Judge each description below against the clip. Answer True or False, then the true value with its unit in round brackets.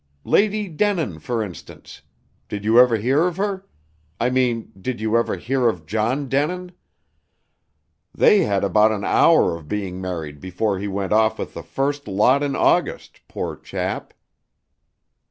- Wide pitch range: True (6.3 semitones)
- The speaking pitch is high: False (115 Hz)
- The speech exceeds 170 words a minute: False (155 wpm)